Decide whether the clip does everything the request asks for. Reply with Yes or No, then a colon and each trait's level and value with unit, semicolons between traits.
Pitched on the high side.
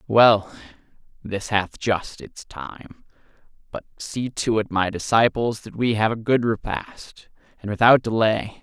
No: low, 110 Hz